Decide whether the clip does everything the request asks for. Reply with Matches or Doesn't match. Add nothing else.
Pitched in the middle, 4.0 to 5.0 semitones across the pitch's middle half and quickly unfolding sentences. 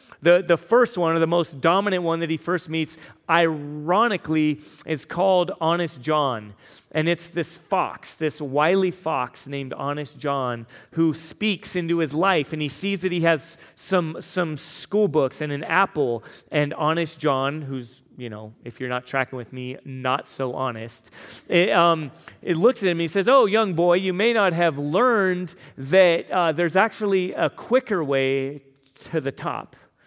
Doesn't match